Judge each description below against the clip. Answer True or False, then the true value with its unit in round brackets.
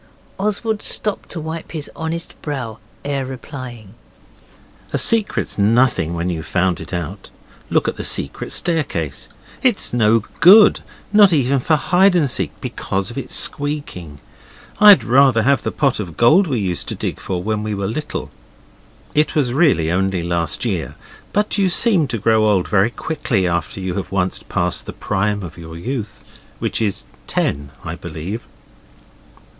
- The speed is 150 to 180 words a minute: True (165 wpm)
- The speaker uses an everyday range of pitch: False (8.4 semitones)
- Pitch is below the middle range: True (115 Hz)